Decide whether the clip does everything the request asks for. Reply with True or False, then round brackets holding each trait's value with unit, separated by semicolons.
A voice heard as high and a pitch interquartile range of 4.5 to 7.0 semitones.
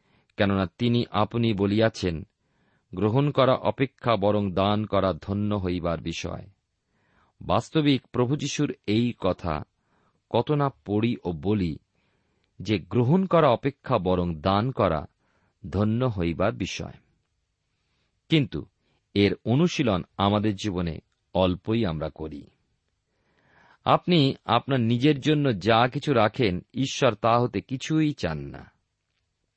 False (105 Hz; 5.3 semitones)